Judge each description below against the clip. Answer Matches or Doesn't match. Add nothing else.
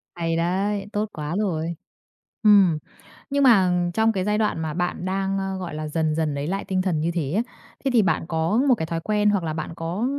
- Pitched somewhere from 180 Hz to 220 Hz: Matches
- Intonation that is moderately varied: Matches